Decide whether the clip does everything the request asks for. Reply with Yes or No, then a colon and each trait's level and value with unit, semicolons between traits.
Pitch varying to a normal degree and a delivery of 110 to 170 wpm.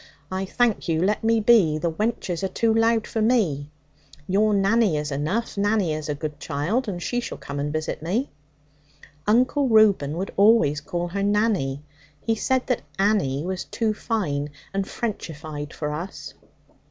No: wide, 6.5 semitones; average, 165 wpm